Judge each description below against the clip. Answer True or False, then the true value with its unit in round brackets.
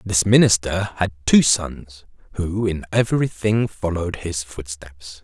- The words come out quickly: False (140 wpm)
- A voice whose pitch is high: False (90 Hz)